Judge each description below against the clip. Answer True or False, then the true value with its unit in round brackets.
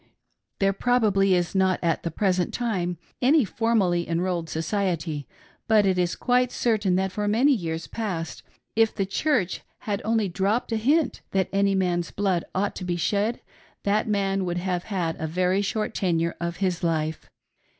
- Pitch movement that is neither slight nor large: True (3.4 semitones)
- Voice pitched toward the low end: False (190 Hz)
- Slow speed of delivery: False (170 wpm)